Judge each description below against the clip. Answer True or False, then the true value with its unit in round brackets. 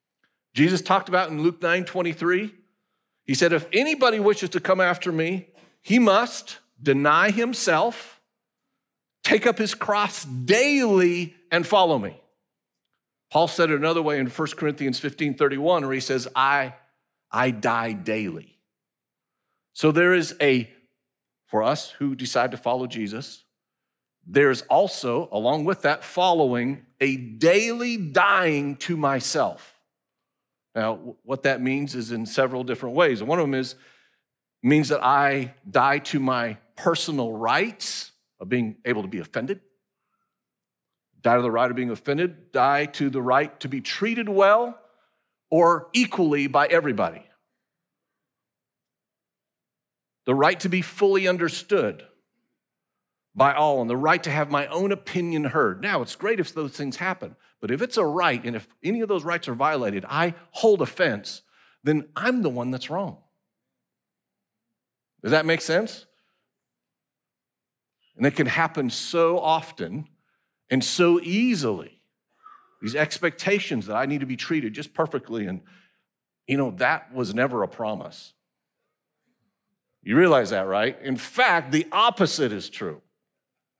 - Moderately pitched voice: True (155 Hz)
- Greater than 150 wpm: False (145 wpm)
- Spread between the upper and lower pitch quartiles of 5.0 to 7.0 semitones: True (5.4 semitones)